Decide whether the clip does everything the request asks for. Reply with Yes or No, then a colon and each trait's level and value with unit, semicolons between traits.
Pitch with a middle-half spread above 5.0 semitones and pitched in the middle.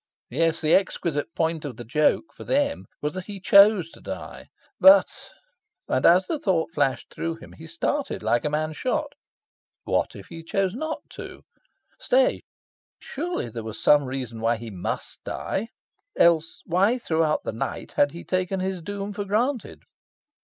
Yes: wide, 5.4 semitones; medium, 170 Hz